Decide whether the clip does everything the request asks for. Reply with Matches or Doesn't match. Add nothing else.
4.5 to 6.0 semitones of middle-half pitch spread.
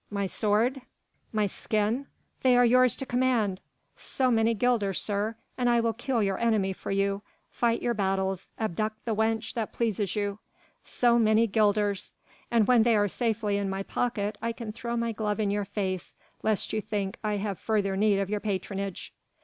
Doesn't match